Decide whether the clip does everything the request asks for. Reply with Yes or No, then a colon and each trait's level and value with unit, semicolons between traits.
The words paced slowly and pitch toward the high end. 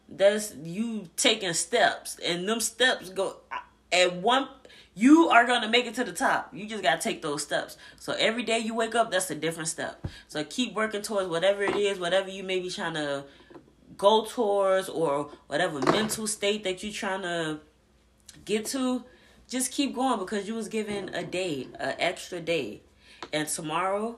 No: average, 180 wpm; high, 205 Hz